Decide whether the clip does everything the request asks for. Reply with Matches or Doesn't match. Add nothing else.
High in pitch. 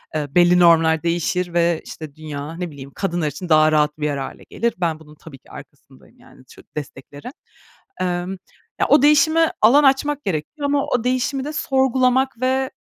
Doesn't match